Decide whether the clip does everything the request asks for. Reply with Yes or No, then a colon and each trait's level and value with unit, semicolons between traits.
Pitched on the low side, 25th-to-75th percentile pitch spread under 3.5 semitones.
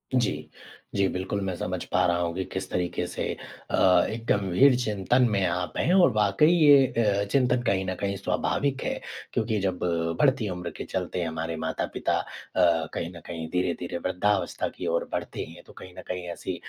No: very low, 95 Hz; average, 4.0 semitones